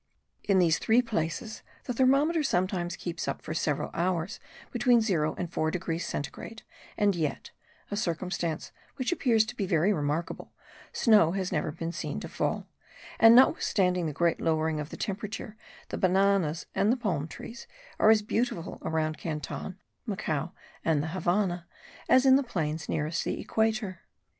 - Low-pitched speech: No, medium, 180 Hz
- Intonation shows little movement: No, average, 5.2 semitones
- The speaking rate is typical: Yes, average, 160 wpm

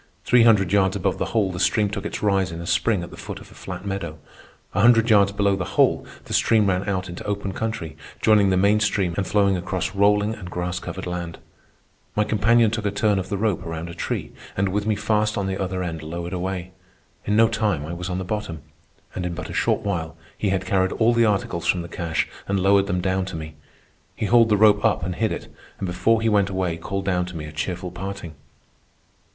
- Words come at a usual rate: No, fast, 235 wpm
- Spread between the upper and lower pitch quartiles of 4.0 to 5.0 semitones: No, average, 2.8 semitones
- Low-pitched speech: Yes, very low, 95 Hz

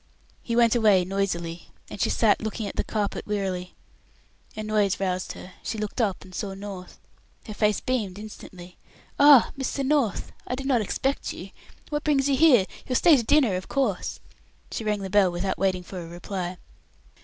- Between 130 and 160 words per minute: No, average, 185 wpm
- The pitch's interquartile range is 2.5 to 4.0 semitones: No, average, 4.5 semitones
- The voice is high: Yes, high, 205 Hz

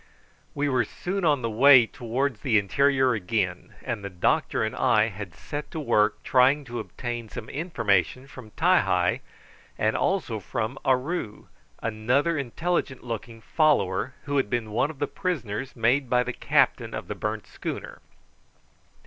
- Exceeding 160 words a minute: No, average, 155 wpm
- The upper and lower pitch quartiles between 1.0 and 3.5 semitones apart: No, average, 4.5 semitones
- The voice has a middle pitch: No, low, 125 Hz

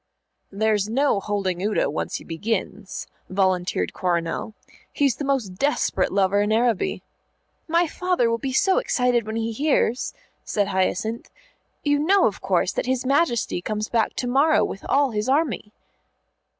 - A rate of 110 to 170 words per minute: Yes, average, 150 wpm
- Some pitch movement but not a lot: No, wide, 5.7 semitones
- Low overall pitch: No, high, 225 Hz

